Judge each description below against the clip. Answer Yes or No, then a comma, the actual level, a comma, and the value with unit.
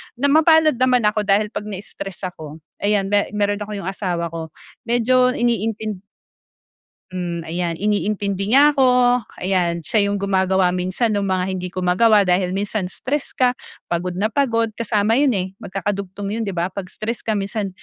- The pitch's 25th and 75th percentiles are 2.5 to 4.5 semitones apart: Yes, average, 3.7 semitones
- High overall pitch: Yes, high, 200 Hz